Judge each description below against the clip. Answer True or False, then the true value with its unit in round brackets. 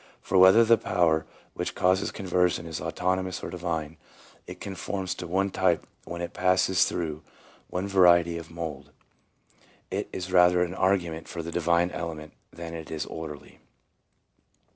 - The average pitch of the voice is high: False (90 Hz)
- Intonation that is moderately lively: False (2.1 semitones)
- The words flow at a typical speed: True (160 wpm)